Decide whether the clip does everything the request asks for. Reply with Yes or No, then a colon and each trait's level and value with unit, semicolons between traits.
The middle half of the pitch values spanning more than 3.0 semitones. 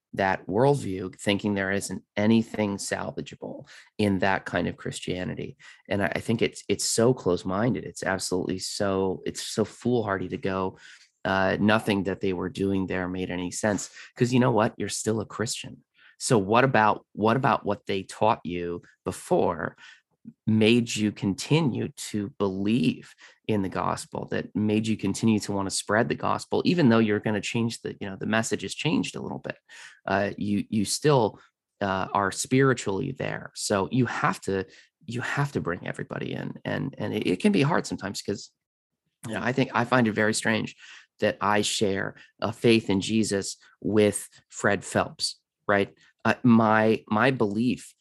No: average, 2.7 semitones